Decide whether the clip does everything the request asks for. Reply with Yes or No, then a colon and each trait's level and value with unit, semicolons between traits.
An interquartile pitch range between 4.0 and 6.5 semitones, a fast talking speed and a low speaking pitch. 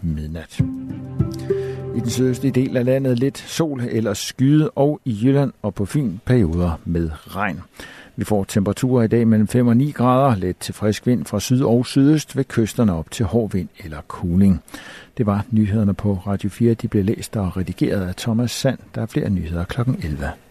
No: average, 4.6 semitones; average, 195 wpm; low, 115 Hz